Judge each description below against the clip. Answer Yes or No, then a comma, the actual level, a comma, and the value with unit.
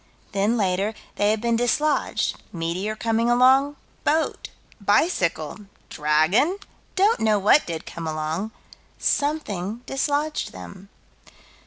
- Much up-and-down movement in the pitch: Yes, wide, 7.2 semitones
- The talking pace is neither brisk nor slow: No, slow, 110 wpm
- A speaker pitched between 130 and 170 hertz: No, high, 215 Hz